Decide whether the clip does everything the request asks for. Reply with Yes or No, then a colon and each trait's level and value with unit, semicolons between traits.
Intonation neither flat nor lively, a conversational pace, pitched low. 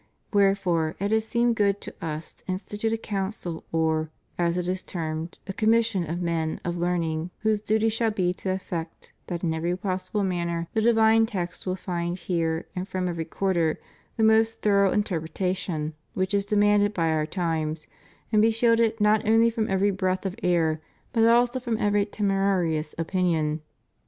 No: average, 3.9 semitones; average, 175 wpm; medium, 185 Hz